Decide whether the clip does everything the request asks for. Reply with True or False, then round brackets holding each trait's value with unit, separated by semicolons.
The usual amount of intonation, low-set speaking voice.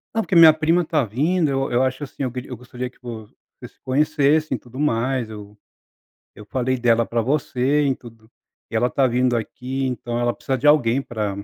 True (3.4 semitones; 130 Hz)